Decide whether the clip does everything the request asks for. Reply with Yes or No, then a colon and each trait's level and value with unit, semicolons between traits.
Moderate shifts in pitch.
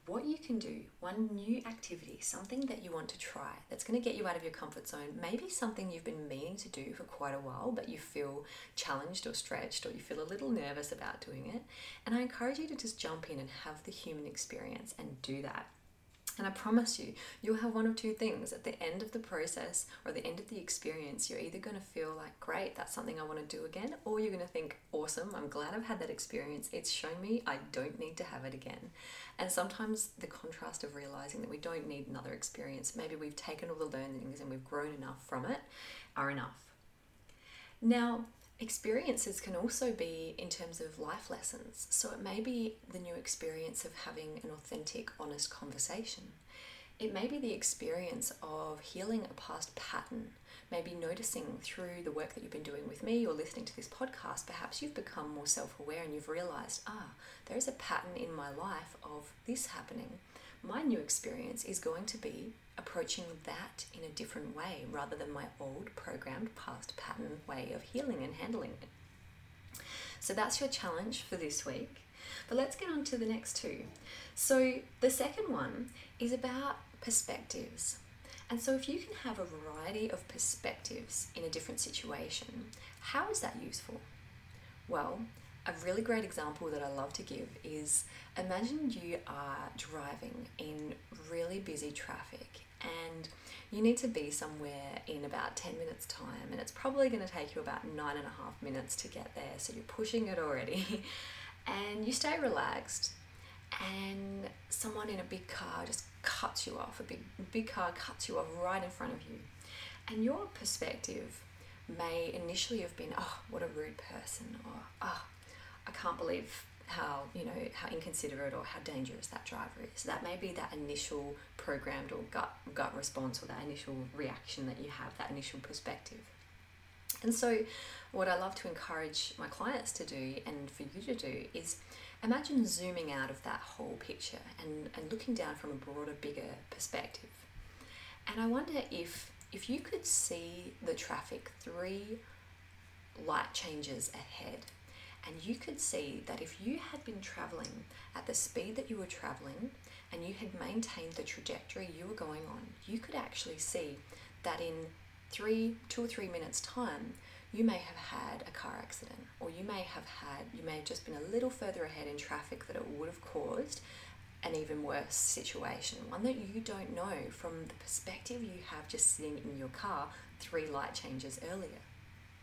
No: wide, 8.7 semitones